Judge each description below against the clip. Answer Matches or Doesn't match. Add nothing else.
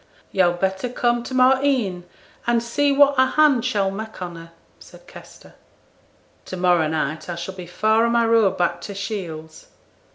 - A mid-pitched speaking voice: Doesn't match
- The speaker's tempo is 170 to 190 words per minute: Matches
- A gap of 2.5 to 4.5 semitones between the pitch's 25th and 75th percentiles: Doesn't match